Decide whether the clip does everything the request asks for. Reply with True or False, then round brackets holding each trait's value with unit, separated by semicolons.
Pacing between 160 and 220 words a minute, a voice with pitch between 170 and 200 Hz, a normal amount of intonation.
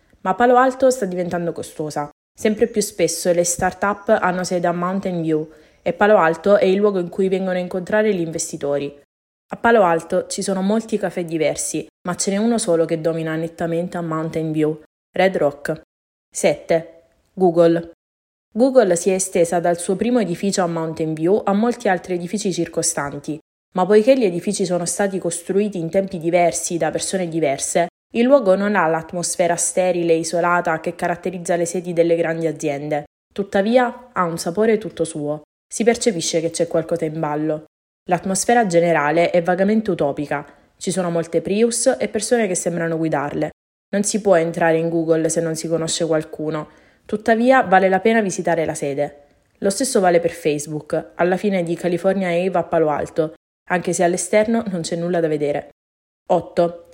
True (170 wpm; 175 Hz; 3.0 semitones)